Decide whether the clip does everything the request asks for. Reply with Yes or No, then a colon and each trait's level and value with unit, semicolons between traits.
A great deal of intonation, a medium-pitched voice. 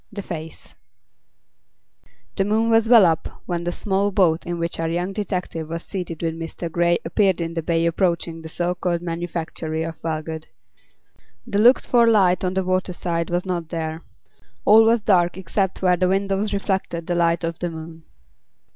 No: narrow, 2.6 semitones; medium, 175 Hz